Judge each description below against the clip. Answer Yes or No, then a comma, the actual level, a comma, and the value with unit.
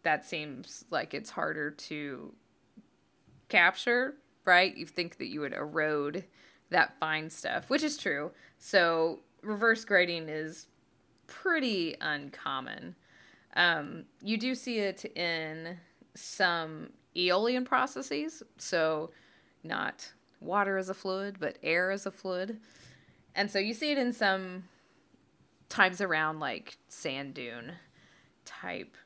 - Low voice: No, medium, 180 Hz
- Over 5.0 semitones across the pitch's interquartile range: Yes, wide, 5.4 semitones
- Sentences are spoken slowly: Yes, slow, 120 wpm